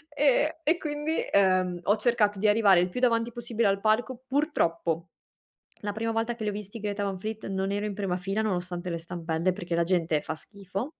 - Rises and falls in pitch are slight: No, average, 4.0 semitones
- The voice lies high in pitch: Yes, high, 205 Hz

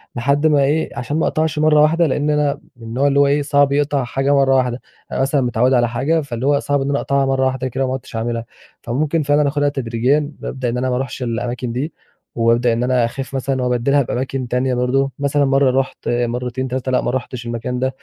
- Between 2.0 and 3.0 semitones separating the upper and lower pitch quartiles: Yes, narrow, 2.4 semitones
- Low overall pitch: Yes, low, 130 Hz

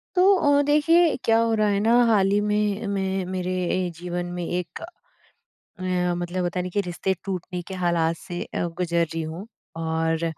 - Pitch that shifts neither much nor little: Yes, average, 3.2 semitones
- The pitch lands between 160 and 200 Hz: Yes, medium, 185 Hz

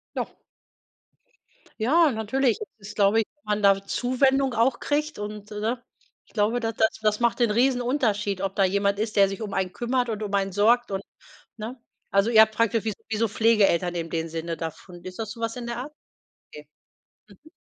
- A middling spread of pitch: Yes, average, 3.2 semitones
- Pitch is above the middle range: Yes, high, 215 Hz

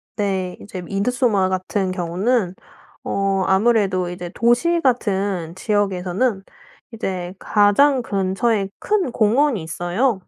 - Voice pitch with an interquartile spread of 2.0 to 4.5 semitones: Yes, average, 4.2 semitones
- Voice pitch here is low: No, high, 200 Hz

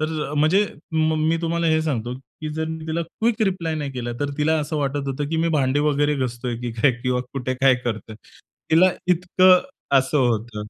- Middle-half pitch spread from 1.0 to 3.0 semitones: No, average, 3.9 semitones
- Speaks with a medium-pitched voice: Yes, medium, 150 Hz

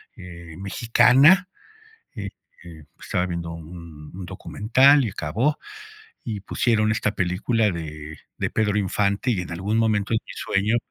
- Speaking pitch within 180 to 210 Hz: No, low, 100 Hz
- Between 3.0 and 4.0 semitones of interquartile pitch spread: No, average, 4.6 semitones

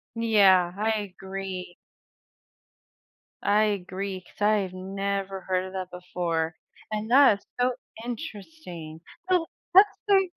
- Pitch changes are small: No, average, 3.0 semitones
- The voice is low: No, high, 195 Hz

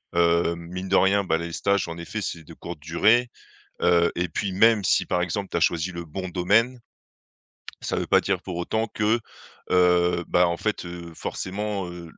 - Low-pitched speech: Yes, very low, 90 Hz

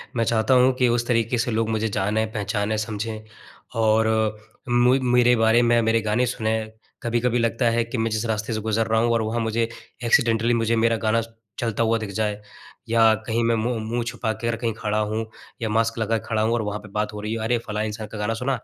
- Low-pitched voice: Yes, low, 115 Hz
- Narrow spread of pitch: Yes, narrow, 1.3 semitones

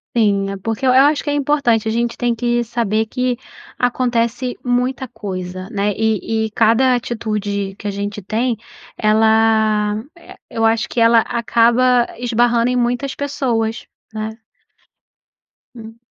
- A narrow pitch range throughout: Yes, narrow, 2.2 semitones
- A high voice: Yes, high, 230 Hz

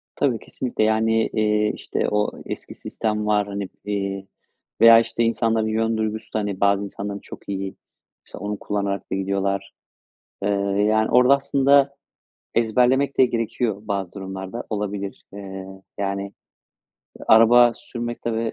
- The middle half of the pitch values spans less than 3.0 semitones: Yes, narrow, 2.6 semitones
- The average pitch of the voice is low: Yes, low, 105 Hz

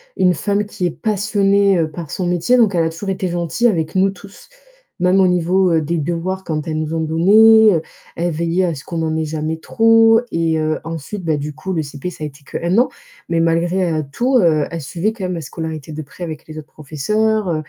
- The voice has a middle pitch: Yes, medium, 170 Hz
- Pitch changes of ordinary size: Yes, average, 3.7 semitones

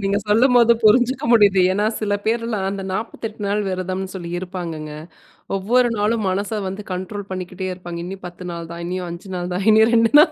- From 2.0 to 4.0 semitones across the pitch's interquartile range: Yes, average, 3.0 semitones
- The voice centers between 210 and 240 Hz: No, high, 195 Hz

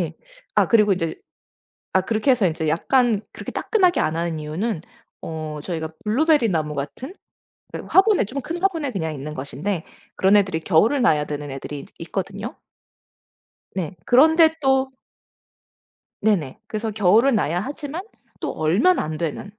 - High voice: Yes, high, 195 Hz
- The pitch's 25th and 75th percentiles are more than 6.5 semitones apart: Yes, wide, 8.6 semitones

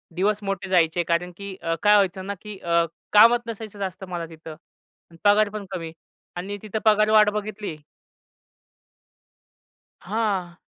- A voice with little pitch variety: No, average, 3.1 semitones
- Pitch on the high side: Yes, high, 200 Hz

